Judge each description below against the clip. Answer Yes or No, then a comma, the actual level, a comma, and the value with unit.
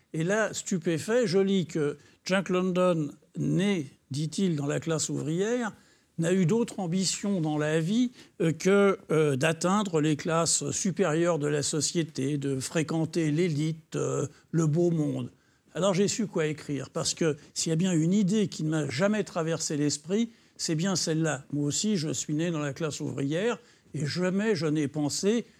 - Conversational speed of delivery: Yes, average, 170 wpm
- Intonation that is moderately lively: Yes, average, 4.1 semitones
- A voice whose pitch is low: No, medium, 165 Hz